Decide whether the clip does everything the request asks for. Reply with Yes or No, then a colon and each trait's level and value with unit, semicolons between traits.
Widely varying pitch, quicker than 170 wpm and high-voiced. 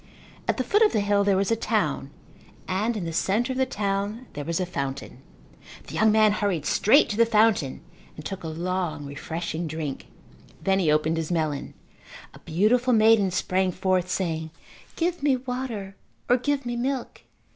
Yes: wide, 5.8 semitones; average, 180 wpm; high, 195 Hz